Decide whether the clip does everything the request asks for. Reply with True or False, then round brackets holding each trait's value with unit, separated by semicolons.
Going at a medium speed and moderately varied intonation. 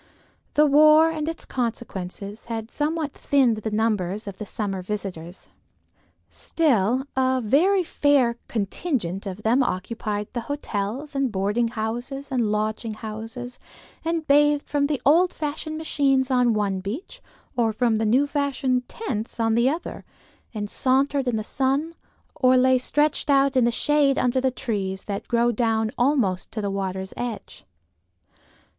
True (150 wpm; 4.8 semitones)